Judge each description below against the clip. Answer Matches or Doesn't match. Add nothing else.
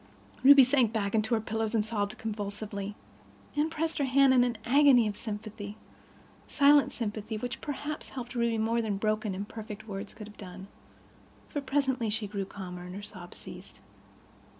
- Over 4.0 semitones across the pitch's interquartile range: Doesn't match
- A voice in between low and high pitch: Doesn't match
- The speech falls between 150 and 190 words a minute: Matches